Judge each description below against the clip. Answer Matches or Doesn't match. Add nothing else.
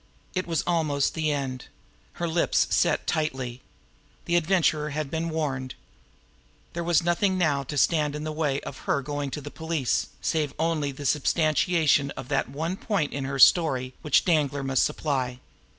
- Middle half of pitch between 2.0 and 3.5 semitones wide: Matches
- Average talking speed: Matches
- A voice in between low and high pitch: Matches